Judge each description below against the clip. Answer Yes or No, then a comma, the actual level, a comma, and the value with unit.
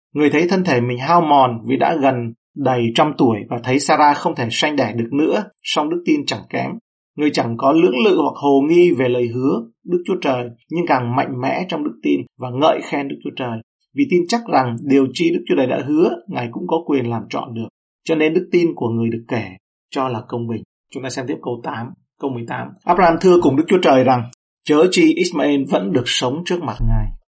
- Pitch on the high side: No, medium, 140 Hz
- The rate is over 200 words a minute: Yes, average, 235 wpm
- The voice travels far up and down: Yes, wide, 6.1 semitones